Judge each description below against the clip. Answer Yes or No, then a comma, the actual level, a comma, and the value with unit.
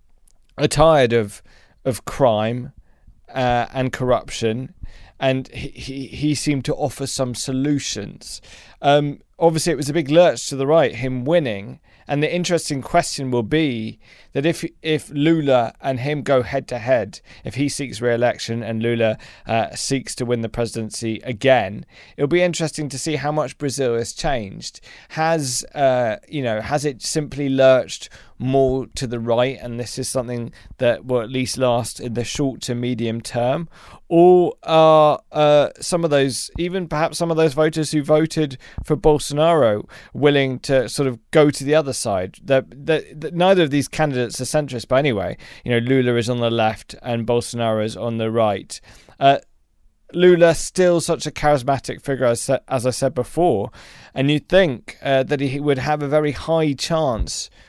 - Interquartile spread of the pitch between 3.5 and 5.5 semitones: Yes, average, 4.0 semitones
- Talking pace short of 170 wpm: No, average, 175 wpm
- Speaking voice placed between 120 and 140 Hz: Yes, low, 135 Hz